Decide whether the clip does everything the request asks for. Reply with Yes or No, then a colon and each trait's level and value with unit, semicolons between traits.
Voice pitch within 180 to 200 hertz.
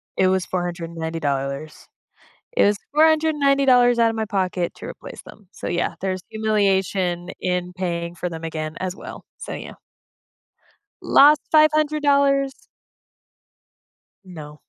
Yes: high, 190 Hz